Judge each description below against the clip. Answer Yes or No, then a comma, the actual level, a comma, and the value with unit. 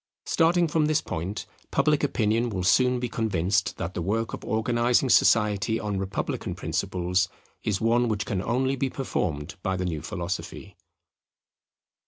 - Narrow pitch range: No, average, 4.7 semitones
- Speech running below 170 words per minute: Yes, average, 150 wpm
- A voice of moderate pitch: No, low, 110 Hz